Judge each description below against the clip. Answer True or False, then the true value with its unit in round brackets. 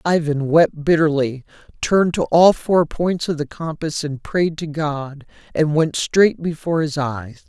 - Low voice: False (155 Hz)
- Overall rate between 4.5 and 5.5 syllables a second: False (4.2 syllables/s)